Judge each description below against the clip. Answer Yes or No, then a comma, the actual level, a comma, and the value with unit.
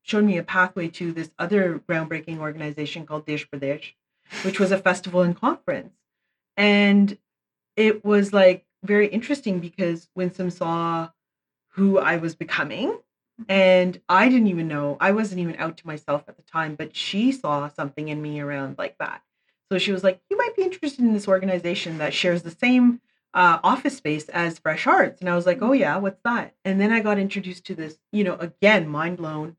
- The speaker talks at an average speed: Yes, average, 195 wpm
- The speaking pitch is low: No, medium, 180 Hz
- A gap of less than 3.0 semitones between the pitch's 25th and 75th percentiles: No, average, 4.2 semitones